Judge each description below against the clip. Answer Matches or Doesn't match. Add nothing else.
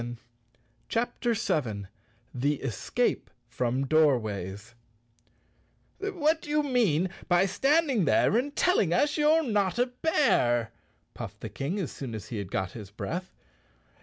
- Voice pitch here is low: Doesn't match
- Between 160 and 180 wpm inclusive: Doesn't match